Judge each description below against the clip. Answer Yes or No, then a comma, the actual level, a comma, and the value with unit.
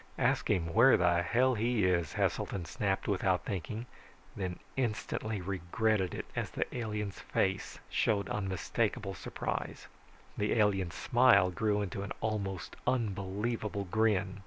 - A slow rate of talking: Yes, slow, 130 wpm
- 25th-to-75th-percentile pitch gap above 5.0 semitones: No, average, 3.0 semitones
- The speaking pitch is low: Yes, low, 100 Hz